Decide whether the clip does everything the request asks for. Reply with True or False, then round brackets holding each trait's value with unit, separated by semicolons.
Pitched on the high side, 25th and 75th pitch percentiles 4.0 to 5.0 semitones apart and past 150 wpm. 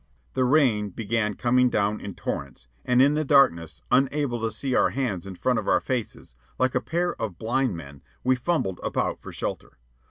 False (120 Hz; 4.7 semitones; 190 wpm)